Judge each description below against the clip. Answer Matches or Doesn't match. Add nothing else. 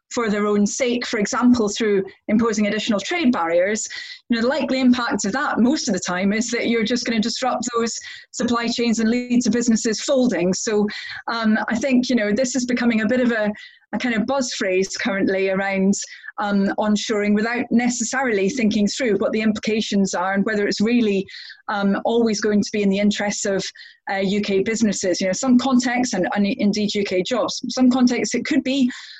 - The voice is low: Doesn't match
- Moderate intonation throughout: Matches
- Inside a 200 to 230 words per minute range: Matches